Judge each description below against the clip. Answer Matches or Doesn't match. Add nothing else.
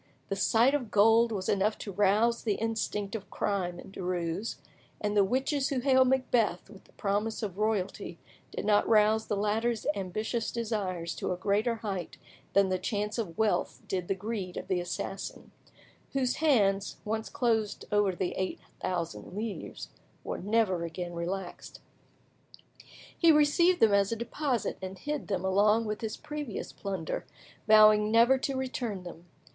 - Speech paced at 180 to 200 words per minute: Doesn't match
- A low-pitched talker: Doesn't match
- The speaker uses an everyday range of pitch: Matches